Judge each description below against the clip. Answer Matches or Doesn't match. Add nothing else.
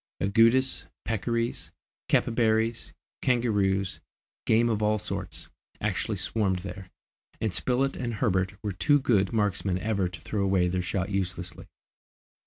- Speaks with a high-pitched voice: Doesn't match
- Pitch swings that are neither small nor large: Matches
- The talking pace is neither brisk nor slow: Doesn't match